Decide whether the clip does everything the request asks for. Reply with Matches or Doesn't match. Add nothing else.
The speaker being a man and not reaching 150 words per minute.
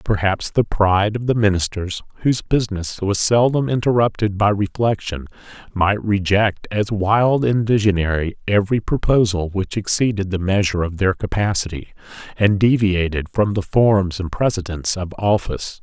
Matches